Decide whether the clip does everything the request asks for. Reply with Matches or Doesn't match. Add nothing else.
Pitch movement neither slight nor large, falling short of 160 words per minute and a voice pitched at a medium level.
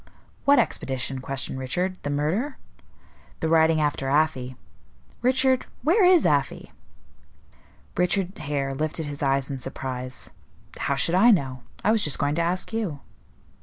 Doesn't match